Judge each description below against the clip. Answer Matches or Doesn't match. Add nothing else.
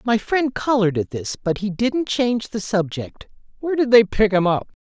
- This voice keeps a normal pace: Doesn't match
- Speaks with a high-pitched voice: Matches